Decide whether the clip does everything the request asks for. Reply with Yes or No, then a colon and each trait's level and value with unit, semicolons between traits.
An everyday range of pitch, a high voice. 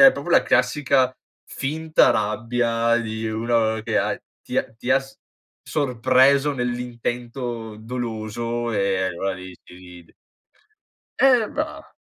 No: average, 3.4 semitones; low, 120 Hz